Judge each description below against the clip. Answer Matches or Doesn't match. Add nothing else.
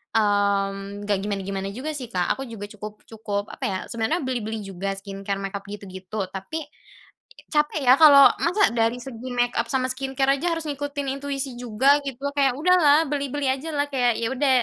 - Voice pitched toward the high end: Matches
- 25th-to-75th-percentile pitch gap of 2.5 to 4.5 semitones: Doesn't match